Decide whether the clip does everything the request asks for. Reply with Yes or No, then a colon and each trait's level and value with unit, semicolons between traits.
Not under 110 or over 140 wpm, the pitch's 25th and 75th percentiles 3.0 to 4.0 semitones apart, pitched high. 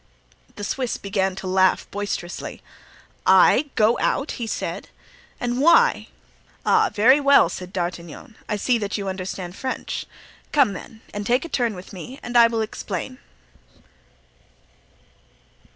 No: slow, 135 wpm; average, 4.9 semitones; high, 215 Hz